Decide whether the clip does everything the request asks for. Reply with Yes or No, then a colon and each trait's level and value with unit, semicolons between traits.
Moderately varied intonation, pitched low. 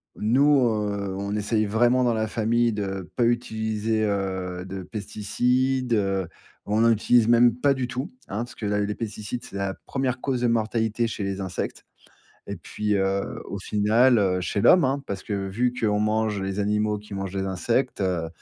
Yes: average, 3.2 semitones; low, 105 Hz